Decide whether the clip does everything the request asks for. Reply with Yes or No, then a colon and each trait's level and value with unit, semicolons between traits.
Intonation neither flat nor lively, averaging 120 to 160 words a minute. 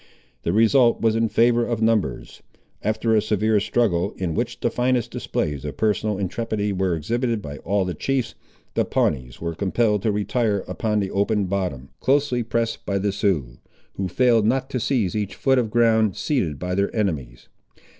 No: average, 3.8 semitones; average, 175 wpm